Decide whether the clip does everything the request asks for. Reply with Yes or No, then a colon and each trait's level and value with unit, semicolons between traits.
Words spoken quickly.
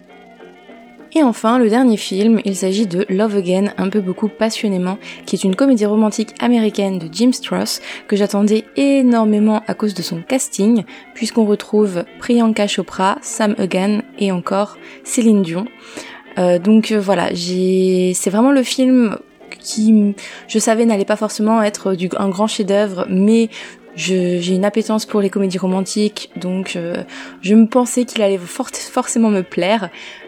No: average, 160 wpm